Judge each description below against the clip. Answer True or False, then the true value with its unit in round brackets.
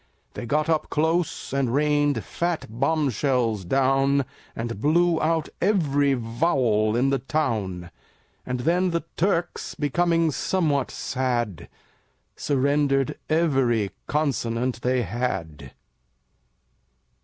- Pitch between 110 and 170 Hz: True (135 Hz)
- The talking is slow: True (100 wpm)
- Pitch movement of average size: True (4.7 semitones)